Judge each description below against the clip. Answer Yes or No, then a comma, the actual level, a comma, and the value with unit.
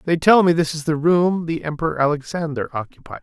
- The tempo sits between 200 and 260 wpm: Yes, fast, 205 wpm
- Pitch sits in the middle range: Yes, medium, 160 Hz